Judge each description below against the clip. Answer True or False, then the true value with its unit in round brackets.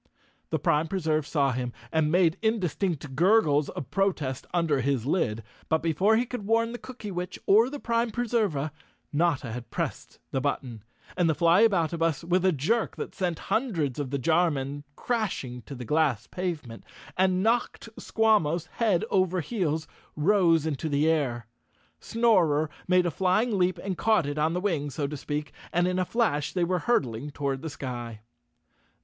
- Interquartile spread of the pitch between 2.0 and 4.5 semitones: False (5.3 semitones)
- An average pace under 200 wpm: True (170 wpm)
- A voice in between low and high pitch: True (165 Hz)